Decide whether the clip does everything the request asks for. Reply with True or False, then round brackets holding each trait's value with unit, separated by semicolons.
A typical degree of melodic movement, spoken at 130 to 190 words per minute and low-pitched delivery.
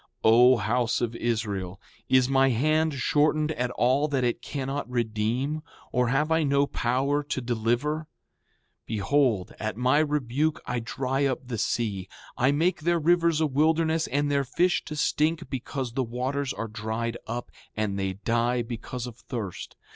True (4.0 semitones; 160 wpm; 130 Hz)